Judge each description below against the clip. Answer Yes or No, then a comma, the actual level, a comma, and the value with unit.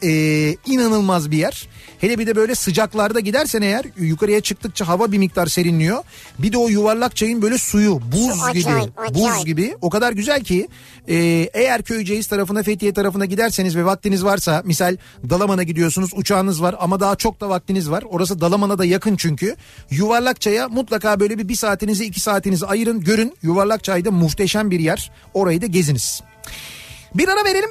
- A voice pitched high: Yes, high, 200 Hz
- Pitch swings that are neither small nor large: Yes, average, 3.8 semitones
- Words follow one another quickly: Yes, fast, 170 wpm